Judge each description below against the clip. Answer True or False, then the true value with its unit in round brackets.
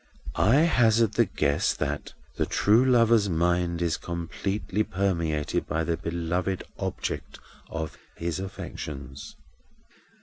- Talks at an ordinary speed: False (110 wpm)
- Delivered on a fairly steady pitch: False (4.4 semitones)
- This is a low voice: True (90 Hz)